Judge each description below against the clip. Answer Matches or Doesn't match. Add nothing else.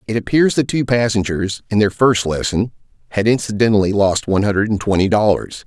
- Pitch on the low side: Matches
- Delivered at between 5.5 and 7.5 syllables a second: Matches